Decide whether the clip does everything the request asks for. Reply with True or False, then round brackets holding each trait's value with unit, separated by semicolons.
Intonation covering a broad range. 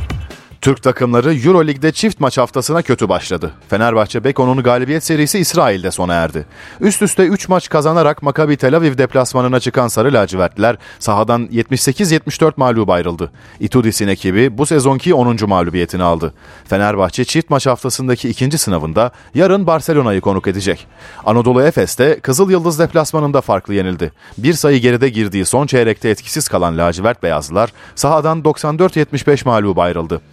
True (7.2 semitones)